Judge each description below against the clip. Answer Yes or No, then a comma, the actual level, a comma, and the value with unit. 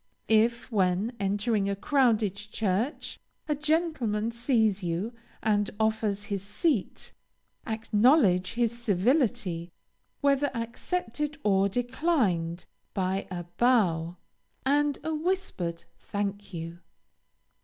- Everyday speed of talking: No, slow, 100 wpm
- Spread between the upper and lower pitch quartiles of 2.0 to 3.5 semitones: No, average, 4.8 semitones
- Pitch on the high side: Yes, high, 220 Hz